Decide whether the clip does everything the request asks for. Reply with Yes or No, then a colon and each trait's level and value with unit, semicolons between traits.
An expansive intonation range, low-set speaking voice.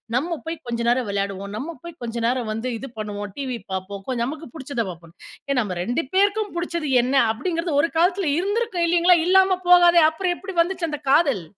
No: wide, 7.1 semitones; very high, 295 Hz